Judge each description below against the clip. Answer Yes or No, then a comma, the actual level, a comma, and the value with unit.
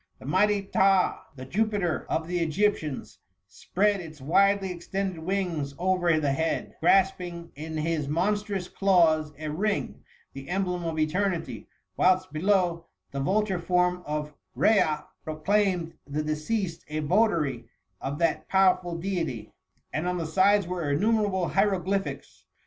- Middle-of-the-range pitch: Yes, medium, 175 Hz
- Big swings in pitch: No, average, 3.9 semitones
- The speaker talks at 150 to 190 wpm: No, slow, 135 wpm